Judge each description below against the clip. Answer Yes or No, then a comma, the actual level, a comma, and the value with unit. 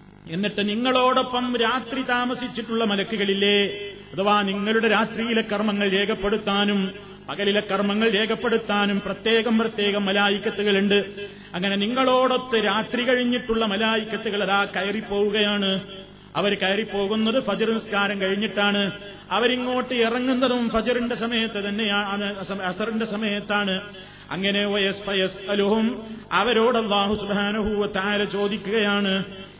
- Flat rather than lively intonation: Yes, narrow, 2.0 semitones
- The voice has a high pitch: Yes, high, 205 Hz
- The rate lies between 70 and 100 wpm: Yes, average, 85 wpm